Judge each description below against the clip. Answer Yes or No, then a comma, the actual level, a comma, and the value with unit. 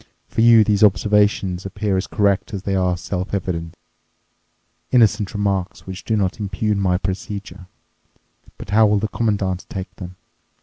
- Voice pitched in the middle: No, low, 100 Hz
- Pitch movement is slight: Yes, narrow, 2.1 semitones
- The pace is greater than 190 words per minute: No, average, 145 wpm